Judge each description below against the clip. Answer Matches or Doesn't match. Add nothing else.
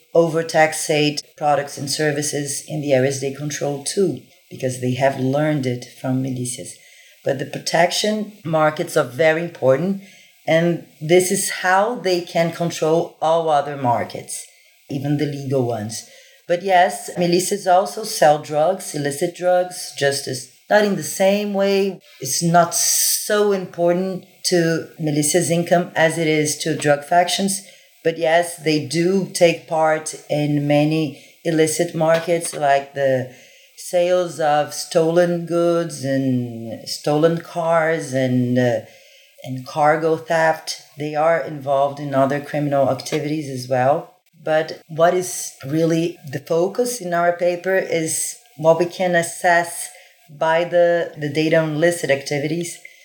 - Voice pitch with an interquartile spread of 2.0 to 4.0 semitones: Matches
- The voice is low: Doesn't match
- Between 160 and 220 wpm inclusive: Doesn't match